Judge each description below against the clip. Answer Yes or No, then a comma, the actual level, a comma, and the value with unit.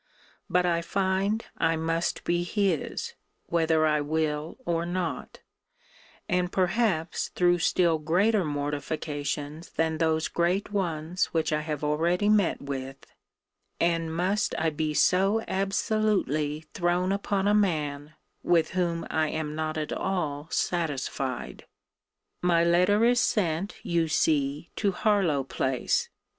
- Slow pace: Yes, slow, 125 wpm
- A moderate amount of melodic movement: Yes, average, 3.3 semitones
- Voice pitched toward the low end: No, medium, 165 Hz